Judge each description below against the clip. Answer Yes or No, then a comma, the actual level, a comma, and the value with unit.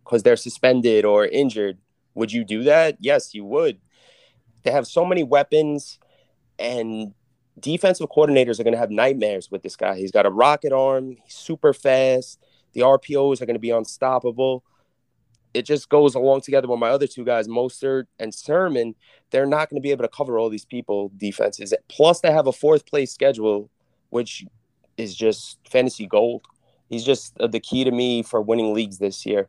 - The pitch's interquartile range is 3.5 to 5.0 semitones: Yes, average, 3.9 semitones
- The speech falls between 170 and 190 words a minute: Yes, average, 185 wpm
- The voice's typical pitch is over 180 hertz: No, low, 130 Hz